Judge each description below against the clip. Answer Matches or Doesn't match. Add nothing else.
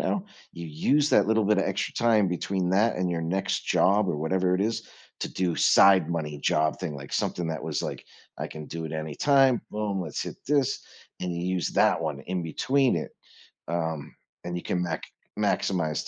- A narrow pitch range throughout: Doesn't match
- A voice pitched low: Matches